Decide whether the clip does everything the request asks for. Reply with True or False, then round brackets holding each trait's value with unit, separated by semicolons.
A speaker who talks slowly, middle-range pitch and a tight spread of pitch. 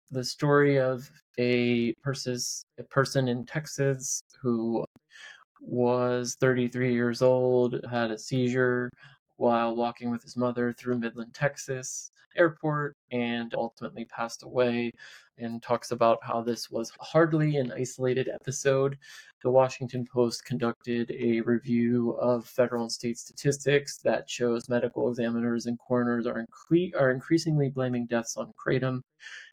False (130 wpm; 125 Hz; 2.2 semitones)